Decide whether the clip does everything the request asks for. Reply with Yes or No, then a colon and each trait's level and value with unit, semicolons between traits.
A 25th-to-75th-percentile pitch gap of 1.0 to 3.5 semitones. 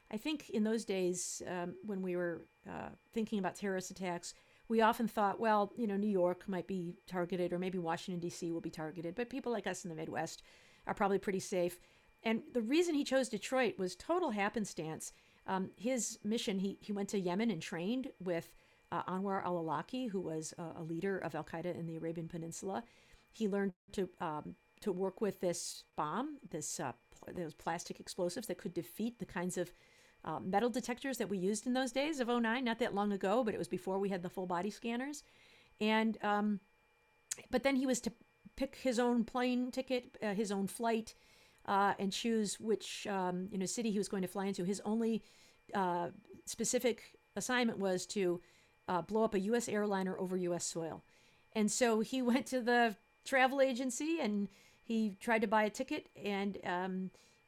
No: average, 4.3 semitones